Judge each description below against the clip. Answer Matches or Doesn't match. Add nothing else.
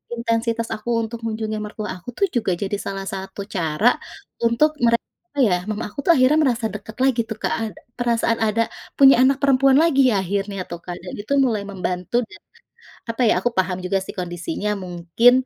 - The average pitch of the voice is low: Doesn't match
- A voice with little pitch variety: Doesn't match